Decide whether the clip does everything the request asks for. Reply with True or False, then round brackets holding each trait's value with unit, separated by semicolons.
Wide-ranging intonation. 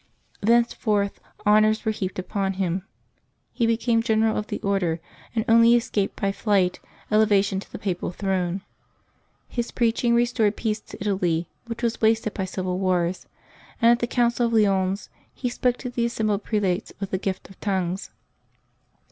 False (3.3 semitones)